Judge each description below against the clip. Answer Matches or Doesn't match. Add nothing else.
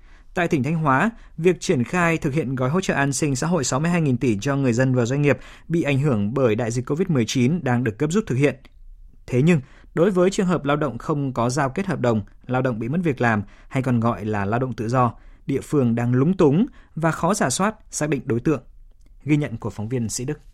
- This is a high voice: Doesn't match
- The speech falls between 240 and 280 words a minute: Matches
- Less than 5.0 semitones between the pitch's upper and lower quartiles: Doesn't match